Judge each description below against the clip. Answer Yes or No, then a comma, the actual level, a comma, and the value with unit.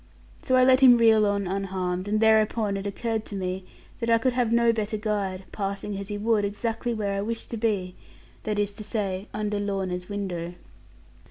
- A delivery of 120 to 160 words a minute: No, average, 195 wpm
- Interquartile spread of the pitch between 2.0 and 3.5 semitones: Yes, narrow, 2.4 semitones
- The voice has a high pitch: Yes, high, 205 Hz